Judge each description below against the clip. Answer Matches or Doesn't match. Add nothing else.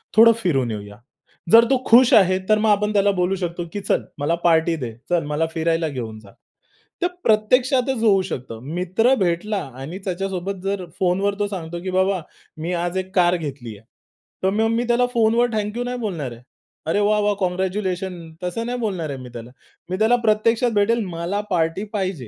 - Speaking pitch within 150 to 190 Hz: Matches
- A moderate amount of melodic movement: Matches